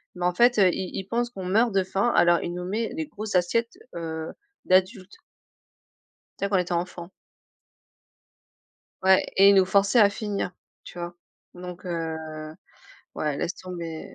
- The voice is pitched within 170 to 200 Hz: Yes, medium, 185 Hz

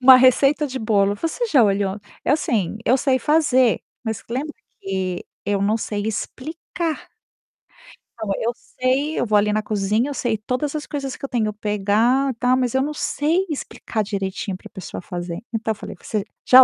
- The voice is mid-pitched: No, high, 235 Hz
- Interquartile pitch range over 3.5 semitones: Yes, average, 4.8 semitones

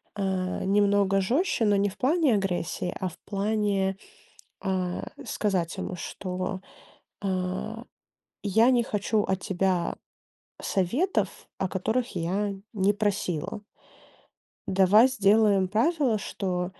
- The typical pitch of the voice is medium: No, high, 195 Hz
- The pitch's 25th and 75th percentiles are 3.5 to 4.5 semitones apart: No, narrow, 2.6 semitones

